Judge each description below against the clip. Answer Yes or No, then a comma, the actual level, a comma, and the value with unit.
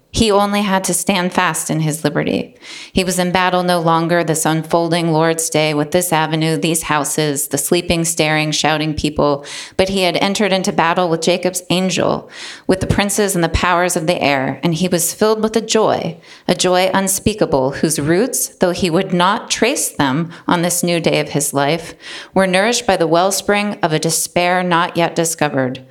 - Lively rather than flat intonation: No, average, 2.7 semitones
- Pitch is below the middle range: No, medium, 175 Hz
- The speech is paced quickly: No, average, 190 wpm